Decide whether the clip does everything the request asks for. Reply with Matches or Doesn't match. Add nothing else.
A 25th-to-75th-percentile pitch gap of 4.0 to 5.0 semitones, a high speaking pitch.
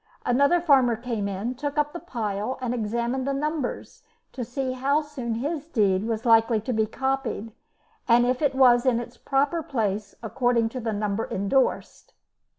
Doesn't match